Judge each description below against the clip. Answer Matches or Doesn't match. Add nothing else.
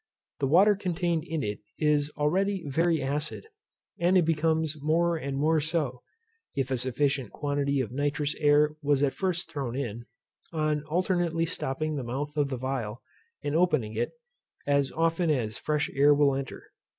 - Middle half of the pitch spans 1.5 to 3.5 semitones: Matches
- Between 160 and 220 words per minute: Matches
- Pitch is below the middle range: Doesn't match